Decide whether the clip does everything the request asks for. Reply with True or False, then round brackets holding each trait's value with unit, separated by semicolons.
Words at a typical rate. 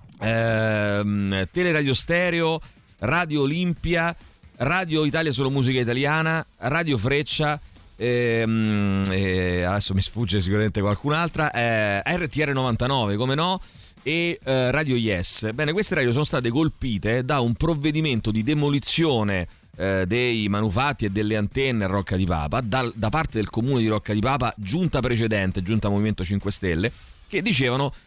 True (140 wpm)